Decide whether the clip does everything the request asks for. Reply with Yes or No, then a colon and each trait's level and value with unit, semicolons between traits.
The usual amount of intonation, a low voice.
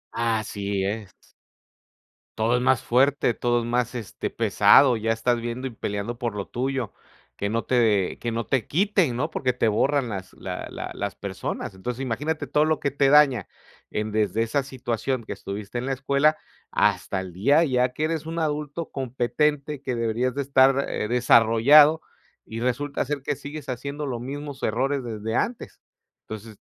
Yes: average, 3.9 semitones; low, 125 Hz